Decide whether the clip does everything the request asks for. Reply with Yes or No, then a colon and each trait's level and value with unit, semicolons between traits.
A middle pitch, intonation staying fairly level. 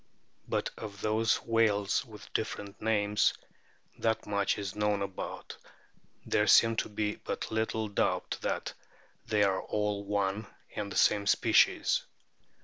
No: low, 105 Hz; narrow, 1.3 semitones